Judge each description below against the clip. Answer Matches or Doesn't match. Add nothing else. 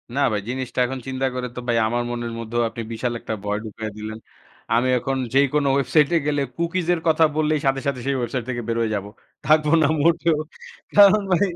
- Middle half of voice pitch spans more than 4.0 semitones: Matches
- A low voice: Matches